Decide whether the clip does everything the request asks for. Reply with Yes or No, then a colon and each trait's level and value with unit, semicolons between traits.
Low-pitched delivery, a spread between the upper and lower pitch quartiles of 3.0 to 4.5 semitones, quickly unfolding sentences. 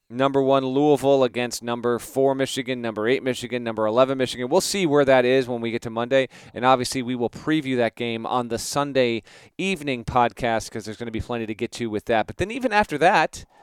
No: low, 125 Hz; narrow, 2.6 semitones; fast, 225 wpm